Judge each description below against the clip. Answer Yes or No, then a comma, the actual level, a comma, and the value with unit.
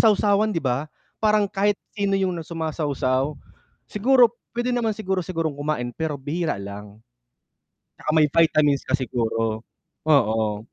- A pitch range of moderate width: No, wide, 7.3 semitones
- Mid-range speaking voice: Yes, medium, 155 Hz